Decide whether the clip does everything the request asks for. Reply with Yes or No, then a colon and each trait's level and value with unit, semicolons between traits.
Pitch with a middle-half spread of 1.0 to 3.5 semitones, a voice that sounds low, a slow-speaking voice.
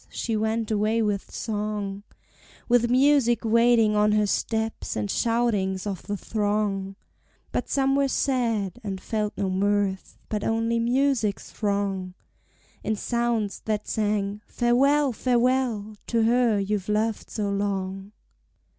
No: average, 2.7 semitones; high, 215 Hz; slow, 130 wpm